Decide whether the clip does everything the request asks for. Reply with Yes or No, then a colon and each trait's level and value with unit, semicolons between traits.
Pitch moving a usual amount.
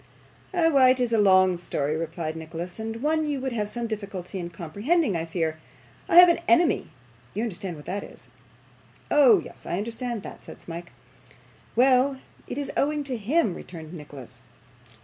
No: wide, 7.5 semitones